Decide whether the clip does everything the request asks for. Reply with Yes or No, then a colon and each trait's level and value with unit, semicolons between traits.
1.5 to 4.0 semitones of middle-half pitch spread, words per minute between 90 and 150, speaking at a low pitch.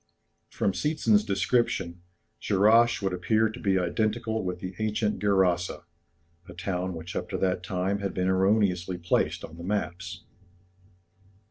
Yes: average, 2.9 semitones; average, 140 wpm; very low, 95 Hz